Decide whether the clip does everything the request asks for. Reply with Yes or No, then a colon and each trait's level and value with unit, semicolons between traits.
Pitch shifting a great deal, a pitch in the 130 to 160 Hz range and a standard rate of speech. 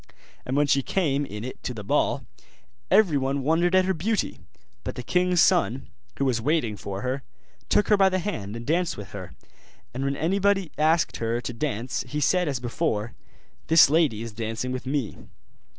Yes: wide, 6.5 semitones; medium, 140 Hz; average, 185 wpm